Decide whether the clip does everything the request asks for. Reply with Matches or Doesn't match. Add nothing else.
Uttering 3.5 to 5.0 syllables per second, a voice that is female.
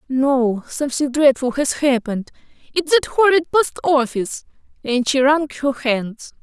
Matches